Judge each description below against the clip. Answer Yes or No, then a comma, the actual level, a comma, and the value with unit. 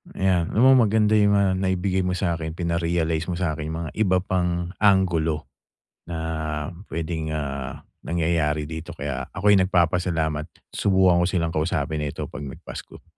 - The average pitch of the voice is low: Yes, very low, 85 Hz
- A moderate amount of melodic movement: Yes, average, 3.0 semitones